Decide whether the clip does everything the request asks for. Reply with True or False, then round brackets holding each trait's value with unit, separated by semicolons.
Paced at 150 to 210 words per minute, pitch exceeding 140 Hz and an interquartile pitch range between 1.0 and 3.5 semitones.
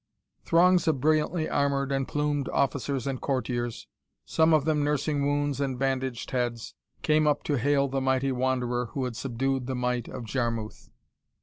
False (165 wpm; 135 Hz; 2.5 semitones)